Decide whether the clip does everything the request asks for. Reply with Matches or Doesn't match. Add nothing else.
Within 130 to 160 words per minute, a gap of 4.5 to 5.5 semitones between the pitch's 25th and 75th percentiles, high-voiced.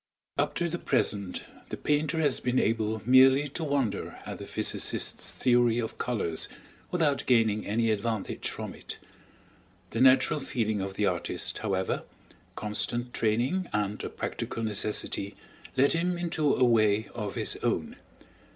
Doesn't match